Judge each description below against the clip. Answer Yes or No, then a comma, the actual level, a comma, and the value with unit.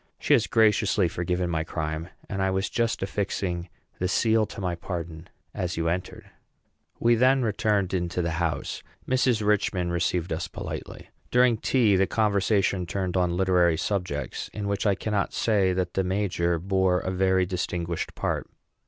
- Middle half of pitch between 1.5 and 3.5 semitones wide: Yes, average, 2.9 semitones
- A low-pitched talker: Yes, very low, 95 Hz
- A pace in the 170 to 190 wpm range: No, average, 160 wpm